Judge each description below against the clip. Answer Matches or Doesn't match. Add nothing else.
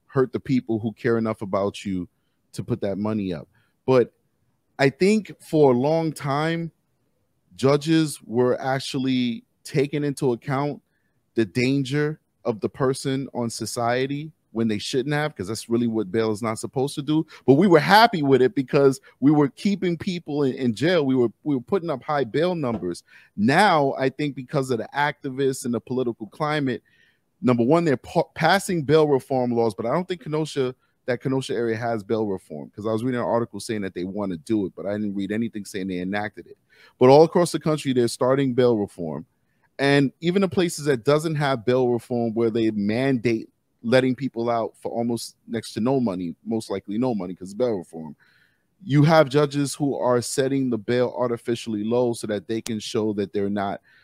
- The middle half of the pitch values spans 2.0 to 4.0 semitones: Doesn't match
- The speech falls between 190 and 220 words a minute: Matches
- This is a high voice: Doesn't match